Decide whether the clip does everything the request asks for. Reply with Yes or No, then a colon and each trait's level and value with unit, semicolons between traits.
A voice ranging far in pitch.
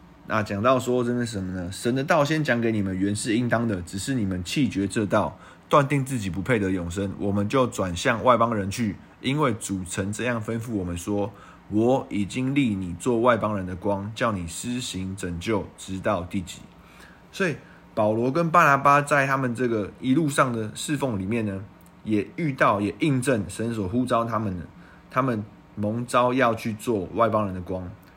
No: average, 4.4 semitones